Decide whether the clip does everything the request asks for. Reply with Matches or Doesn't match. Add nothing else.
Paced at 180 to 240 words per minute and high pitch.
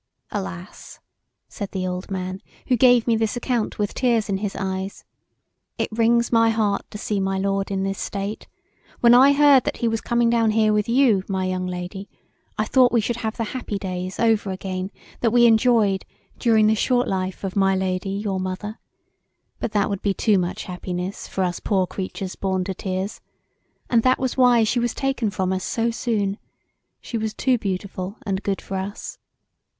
Matches